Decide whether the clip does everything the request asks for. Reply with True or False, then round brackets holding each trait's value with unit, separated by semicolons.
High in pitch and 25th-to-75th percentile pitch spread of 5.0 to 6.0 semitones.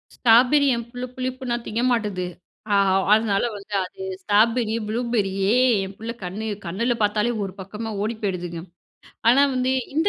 False (225 Hz; 3.5 semitones)